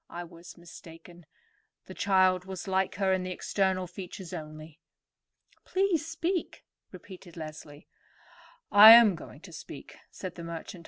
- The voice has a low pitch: No, medium, 185 Hz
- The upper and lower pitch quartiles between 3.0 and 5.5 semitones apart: No, narrow, 2.6 semitones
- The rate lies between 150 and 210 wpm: No, average, 140 wpm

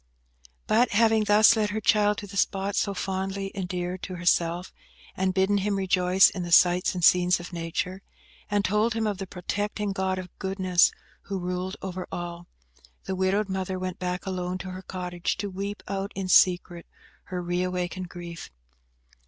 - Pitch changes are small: Yes, narrow, 1.7 semitones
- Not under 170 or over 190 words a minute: Yes, average, 175 wpm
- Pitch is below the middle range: No, medium, 185 Hz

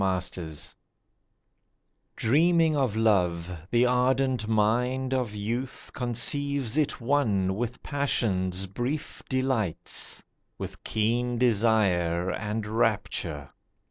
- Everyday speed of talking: No, slow, 90 wpm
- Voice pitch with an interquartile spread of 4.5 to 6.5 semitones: Yes, average, 5.0 semitones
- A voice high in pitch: No, low, 115 Hz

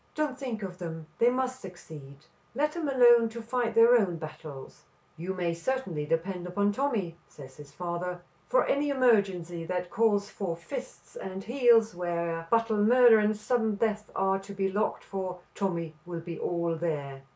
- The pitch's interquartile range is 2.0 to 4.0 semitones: No, wide, 5.4 semitones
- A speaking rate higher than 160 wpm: Yes, average, 170 wpm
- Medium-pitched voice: No, high, 195 Hz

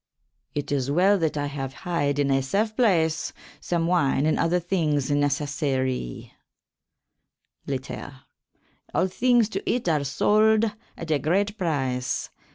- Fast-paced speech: No, slow, 135 wpm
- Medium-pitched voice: Yes, medium, 155 Hz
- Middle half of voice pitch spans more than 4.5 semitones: Yes, average, 5.1 semitones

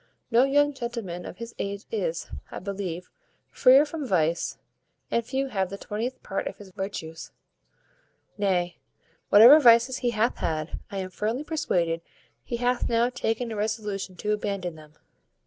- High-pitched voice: Yes, high, 215 Hz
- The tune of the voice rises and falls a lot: No, average, 4.7 semitones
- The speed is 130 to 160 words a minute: Yes, average, 155 wpm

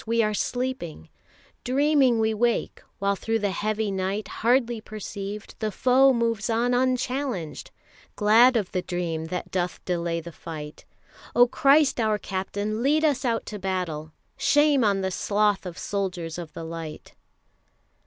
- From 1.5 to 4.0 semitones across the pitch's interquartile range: No, average, 4.9 semitones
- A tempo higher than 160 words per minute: No, average, 150 wpm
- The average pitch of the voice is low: No, high, 215 Hz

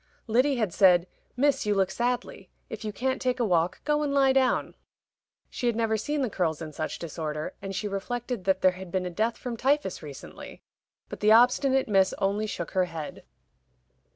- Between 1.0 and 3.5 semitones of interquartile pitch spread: No, wide, 5.4 semitones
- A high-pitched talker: Yes, high, 215 Hz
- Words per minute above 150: Yes, average, 195 wpm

